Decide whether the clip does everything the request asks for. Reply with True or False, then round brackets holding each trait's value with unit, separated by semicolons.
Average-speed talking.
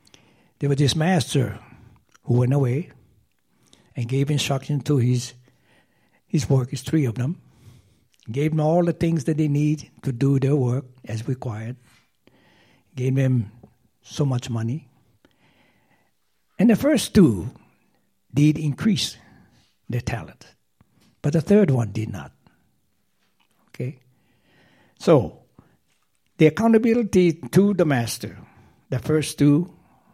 False (120 wpm)